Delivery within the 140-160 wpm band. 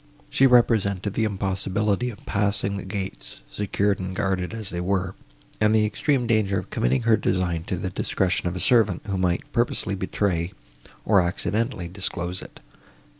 No: average, 170 wpm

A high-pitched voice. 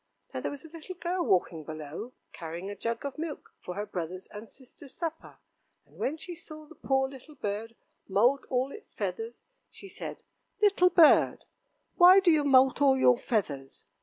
Yes: very high, 265 Hz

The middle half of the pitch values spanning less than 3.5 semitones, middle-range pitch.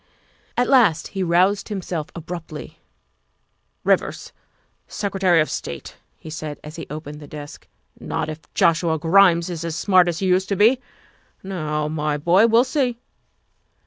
No: average, 3.9 semitones; medium, 170 Hz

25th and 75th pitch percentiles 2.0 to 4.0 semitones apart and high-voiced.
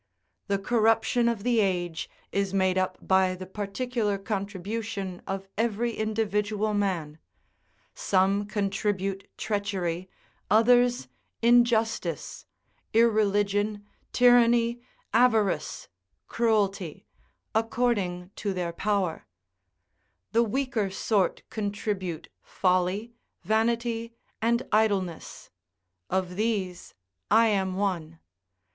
Yes: average, 3.1 semitones; high, 205 Hz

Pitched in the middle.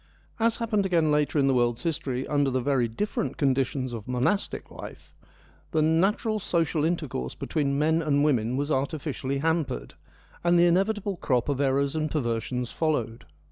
Yes: medium, 145 Hz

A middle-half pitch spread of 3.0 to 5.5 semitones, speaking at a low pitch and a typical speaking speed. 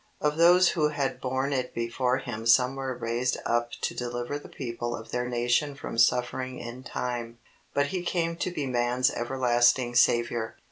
No: narrow, 2.5 semitones; low, 125 Hz; average, 175 wpm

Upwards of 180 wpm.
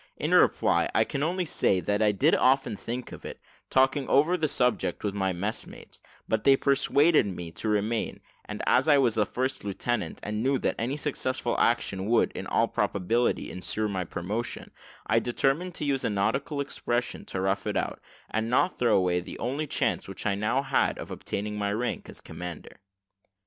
Yes: average, 190 wpm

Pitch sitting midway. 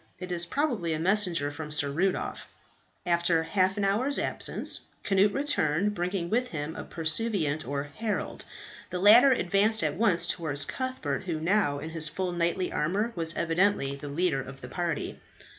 Yes: medium, 175 Hz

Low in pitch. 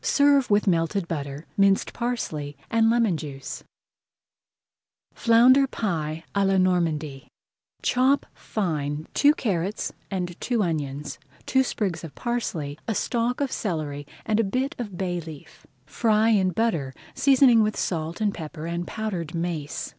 No: high, 190 Hz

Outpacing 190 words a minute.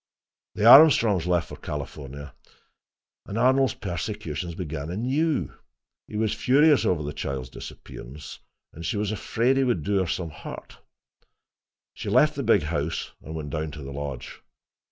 No: average, 155 wpm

